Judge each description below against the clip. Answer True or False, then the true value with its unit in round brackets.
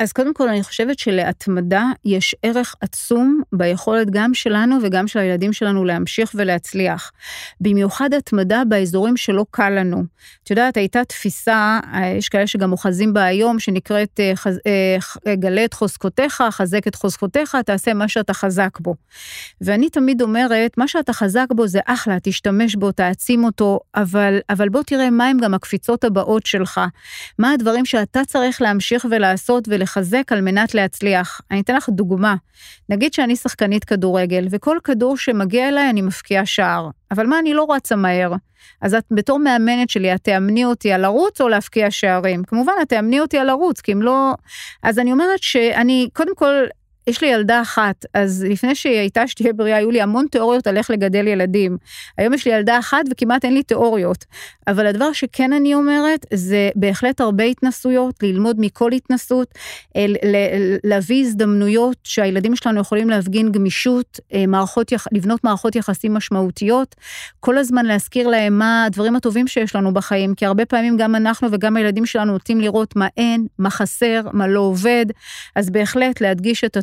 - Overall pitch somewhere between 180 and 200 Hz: False (220 Hz)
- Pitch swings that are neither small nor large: True (3.6 semitones)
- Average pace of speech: False (165 wpm)